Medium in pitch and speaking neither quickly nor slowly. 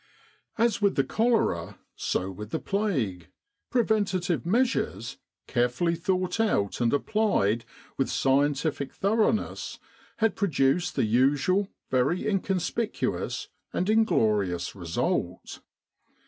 No: medium, 165 Hz; slow, 100 wpm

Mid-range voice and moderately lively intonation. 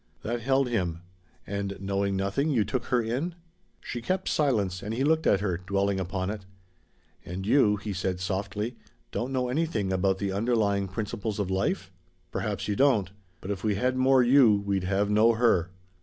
No: low, 105 Hz; average, 4.0 semitones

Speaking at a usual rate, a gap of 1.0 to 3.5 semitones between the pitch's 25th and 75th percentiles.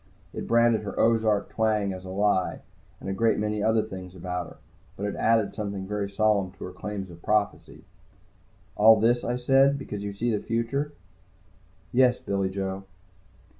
Yes: average, 170 wpm; average, 2.8 semitones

